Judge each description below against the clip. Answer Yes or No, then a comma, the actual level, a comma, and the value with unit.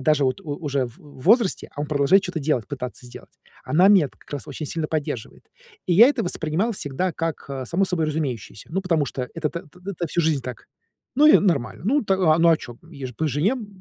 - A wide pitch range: No, average, 4.6 semitones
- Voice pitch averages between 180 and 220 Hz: No, medium, 155 Hz